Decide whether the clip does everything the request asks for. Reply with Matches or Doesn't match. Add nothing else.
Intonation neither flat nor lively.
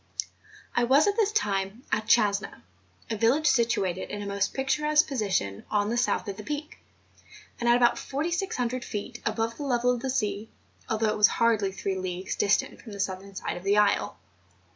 Matches